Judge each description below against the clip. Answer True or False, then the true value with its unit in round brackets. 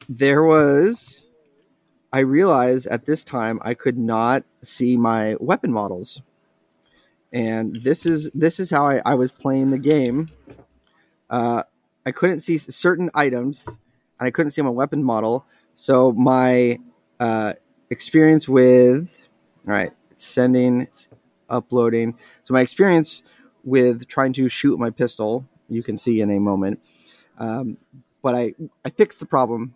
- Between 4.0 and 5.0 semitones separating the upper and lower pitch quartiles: False (3.3 semitones)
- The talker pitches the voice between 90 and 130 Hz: True (125 Hz)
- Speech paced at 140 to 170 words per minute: True (145 wpm)